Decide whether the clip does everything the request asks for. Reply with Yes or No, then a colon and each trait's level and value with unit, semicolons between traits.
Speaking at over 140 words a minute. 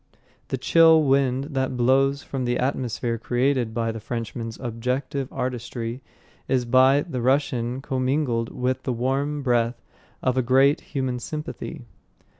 No: slow, 135 wpm